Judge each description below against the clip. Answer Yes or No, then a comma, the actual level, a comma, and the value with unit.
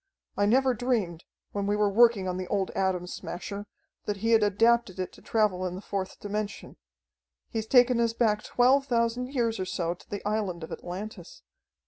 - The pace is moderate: Yes, average, 185 wpm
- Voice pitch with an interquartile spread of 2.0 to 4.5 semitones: Yes, average, 3.6 semitones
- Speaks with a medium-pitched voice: No, high, 210 Hz